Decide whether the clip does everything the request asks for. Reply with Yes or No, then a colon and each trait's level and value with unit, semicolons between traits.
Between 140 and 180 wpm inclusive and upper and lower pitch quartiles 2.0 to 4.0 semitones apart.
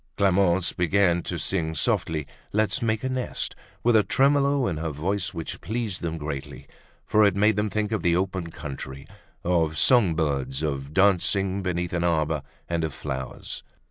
No: average, 165 wpm; average, 4.5 semitones